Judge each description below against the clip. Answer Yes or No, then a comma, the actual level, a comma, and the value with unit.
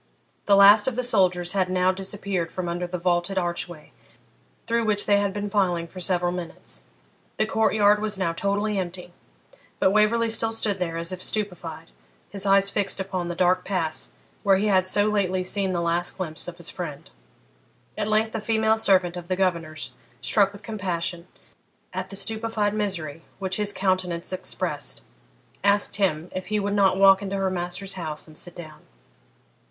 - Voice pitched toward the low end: No, high, 190 Hz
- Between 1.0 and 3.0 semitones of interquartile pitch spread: Yes, narrow, 2.6 semitones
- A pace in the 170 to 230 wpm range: Yes, average, 180 wpm